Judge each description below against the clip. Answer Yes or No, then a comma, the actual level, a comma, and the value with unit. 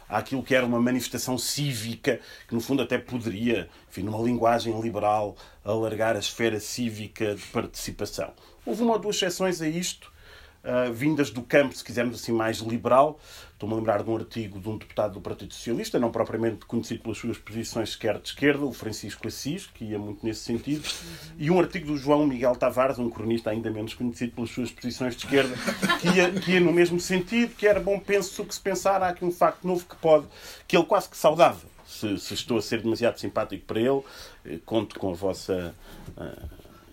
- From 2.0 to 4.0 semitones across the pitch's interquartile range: No, average, 5.2 semitones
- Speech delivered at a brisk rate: Yes, fast, 200 wpm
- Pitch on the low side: Yes, low, 120 Hz